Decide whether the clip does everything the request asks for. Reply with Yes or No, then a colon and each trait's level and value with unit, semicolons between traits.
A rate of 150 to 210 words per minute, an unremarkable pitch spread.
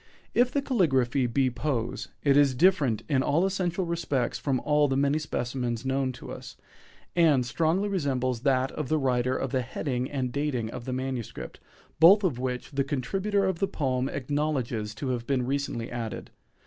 Yes: average, 175 wpm; average, 3.6 semitones